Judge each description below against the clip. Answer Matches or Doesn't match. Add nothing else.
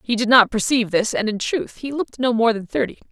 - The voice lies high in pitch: Matches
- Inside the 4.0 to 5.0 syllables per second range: Doesn't match